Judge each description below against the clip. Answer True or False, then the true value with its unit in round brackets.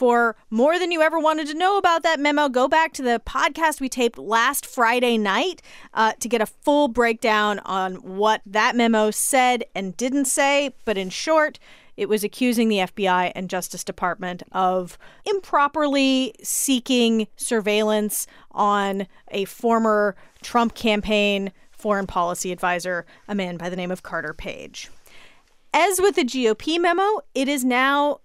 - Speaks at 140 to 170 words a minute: True (155 wpm)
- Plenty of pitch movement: True (6.0 semitones)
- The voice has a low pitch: False (230 Hz)